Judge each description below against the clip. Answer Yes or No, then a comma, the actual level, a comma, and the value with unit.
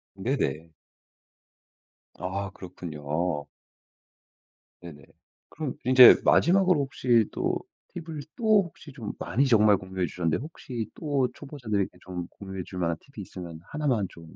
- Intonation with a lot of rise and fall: Yes, wide, 7.9 semitones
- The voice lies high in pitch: No, low, 105 Hz